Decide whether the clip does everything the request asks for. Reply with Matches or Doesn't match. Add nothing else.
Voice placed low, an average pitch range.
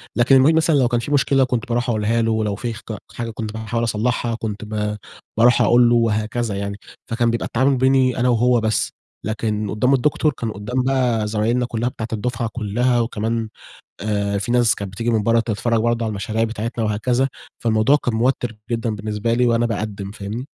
Doesn't match